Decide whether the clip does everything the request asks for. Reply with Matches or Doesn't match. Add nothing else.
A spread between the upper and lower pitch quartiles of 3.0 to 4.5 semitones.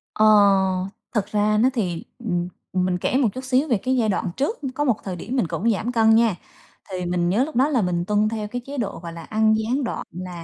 Doesn't match